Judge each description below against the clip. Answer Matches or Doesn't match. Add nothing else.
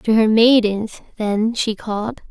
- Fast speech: Doesn't match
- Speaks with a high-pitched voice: Matches